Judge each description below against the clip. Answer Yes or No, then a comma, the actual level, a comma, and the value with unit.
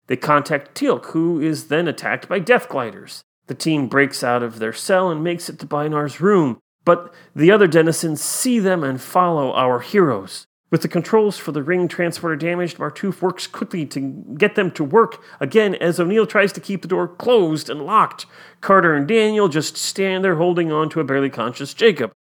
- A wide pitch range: No, average, 4.3 semitones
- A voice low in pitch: No, medium, 170 Hz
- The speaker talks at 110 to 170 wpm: No, average, 195 wpm